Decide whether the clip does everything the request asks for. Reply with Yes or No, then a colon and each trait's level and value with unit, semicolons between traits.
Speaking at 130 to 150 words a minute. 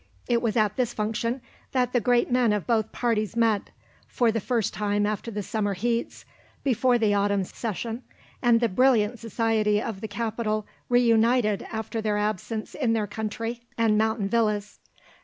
No: average, 165 wpm